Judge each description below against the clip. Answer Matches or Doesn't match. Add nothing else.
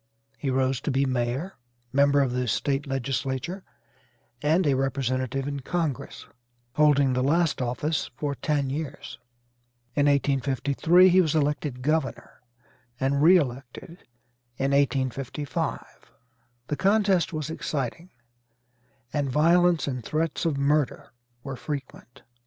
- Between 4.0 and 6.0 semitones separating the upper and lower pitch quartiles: Doesn't match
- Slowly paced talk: Matches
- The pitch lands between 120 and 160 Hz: Matches